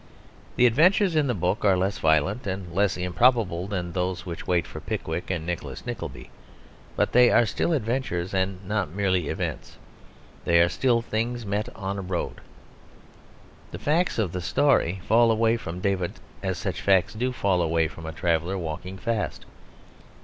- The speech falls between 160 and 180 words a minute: Yes, average, 170 wpm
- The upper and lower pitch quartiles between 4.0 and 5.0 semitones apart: Yes, average, 4.5 semitones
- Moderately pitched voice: No, very low, 95 Hz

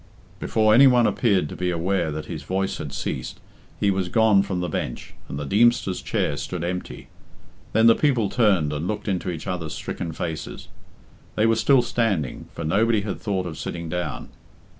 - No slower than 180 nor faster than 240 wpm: Yes, average, 185 wpm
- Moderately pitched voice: No, very low, 95 Hz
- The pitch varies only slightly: No, average, 4.7 semitones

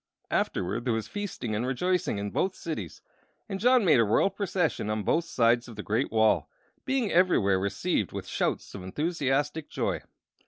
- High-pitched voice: No, low, 135 Hz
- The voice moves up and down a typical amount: No, wide, 9.0 semitones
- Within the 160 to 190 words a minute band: Yes, average, 170 wpm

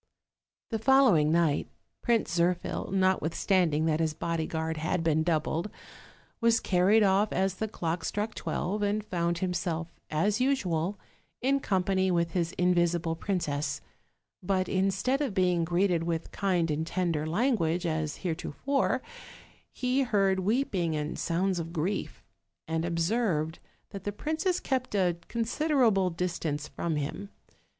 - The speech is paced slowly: Yes, slow, 130 wpm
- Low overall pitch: No, medium, 180 Hz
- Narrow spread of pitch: No, average, 4.0 semitones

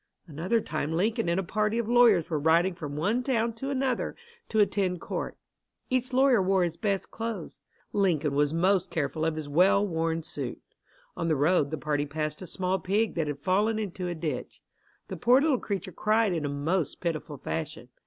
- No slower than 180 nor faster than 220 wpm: Yes, average, 195 wpm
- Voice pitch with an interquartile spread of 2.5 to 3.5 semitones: No, wide, 5.4 semitones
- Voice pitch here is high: No, medium, 180 Hz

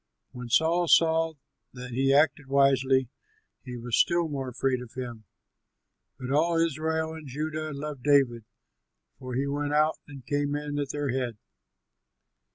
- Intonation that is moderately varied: Yes, average, 3.3 semitones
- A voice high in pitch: No, medium, 140 Hz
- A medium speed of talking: Yes, average, 150 wpm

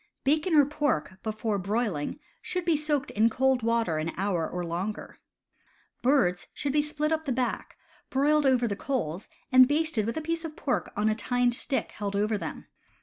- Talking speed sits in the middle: Yes, average, 180 wpm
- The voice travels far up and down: Yes, wide, 6.2 semitones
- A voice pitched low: No, high, 245 Hz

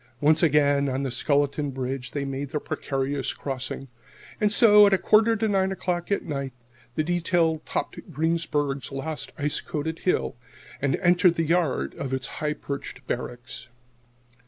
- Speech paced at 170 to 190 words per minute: No, average, 160 wpm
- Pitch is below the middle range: No, medium, 150 Hz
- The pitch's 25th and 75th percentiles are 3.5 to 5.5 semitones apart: Yes, average, 4.2 semitones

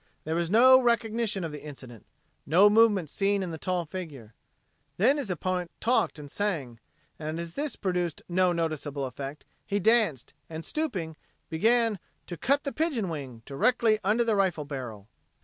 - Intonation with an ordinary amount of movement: No, wide, 6.6 semitones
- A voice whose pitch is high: No, medium, 180 Hz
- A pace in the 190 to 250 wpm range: No, average, 160 wpm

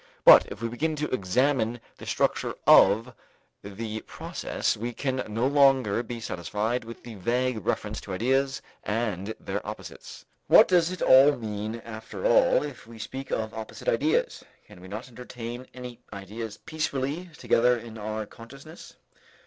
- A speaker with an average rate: Yes, average, 150 wpm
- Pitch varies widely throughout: No, average, 3.5 semitones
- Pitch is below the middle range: Yes, low, 115 Hz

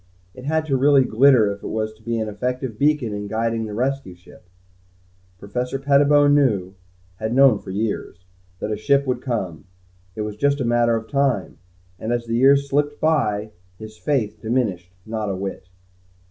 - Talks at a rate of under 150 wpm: No, average, 180 wpm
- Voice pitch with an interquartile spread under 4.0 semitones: No, average, 4.6 semitones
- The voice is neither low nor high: No, low, 115 Hz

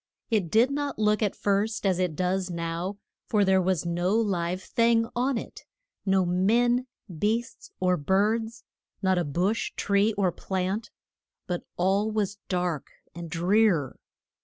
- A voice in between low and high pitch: No, high, 195 Hz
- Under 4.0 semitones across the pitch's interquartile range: Yes, average, 3.5 semitones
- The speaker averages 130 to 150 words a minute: Yes, average, 145 wpm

